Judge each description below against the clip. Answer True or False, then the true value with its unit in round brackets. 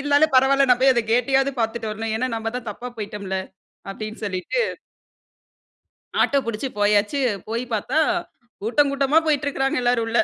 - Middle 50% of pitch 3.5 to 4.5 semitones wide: True (4.0 semitones)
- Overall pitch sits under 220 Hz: False (240 Hz)